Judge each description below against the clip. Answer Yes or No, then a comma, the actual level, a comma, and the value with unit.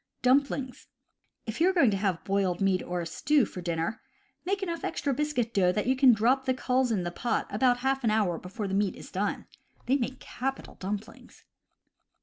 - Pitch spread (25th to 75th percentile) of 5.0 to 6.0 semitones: Yes, wide, 5.4 semitones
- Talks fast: Yes, fast, 210 wpm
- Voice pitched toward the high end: Yes, high, 230 Hz